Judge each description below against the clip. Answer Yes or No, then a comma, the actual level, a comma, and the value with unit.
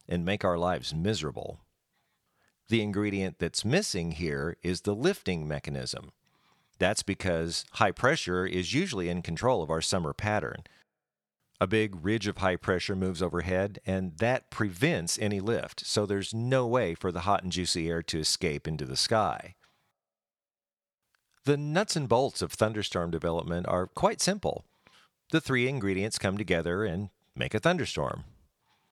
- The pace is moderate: Yes, average, 150 wpm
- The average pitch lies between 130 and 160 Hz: No, very low, 95 Hz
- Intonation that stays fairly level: No, average, 3.8 semitones